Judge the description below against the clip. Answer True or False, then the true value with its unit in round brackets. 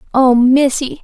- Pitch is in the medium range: False (260 Hz)